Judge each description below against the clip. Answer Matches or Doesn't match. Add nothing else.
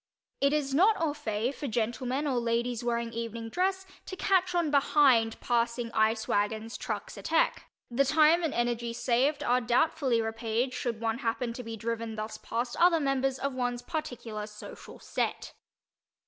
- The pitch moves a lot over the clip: Doesn't match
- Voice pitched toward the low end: Doesn't match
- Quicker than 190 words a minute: Doesn't match